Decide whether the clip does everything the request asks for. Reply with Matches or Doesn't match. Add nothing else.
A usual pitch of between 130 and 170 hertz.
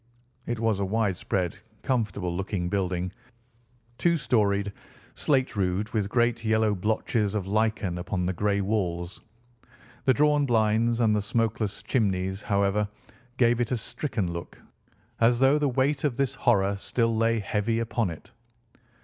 Doesn't match